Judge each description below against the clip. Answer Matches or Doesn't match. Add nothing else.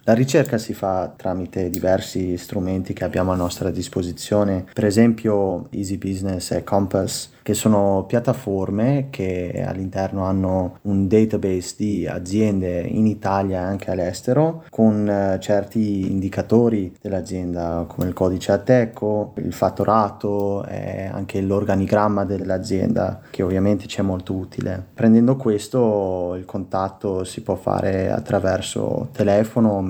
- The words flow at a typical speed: Matches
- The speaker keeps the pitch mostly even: Matches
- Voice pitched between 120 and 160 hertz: Doesn't match